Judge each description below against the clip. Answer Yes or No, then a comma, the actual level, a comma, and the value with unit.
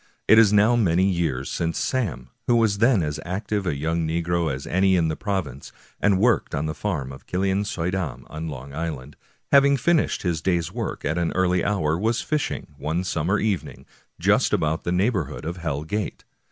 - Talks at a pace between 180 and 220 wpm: Yes, average, 195 wpm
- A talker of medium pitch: No, very low, 90 Hz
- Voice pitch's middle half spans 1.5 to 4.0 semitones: No, average, 4.6 semitones